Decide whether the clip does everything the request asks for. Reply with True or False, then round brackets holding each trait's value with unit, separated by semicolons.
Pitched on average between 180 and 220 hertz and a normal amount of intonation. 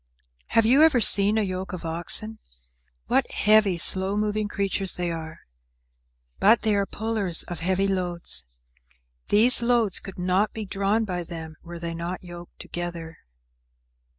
True (190 Hz; 3.5 semitones)